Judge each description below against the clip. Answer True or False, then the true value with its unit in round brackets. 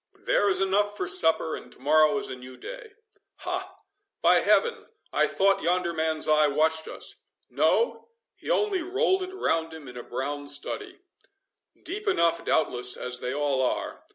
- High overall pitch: False (170 Hz)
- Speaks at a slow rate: False (155 wpm)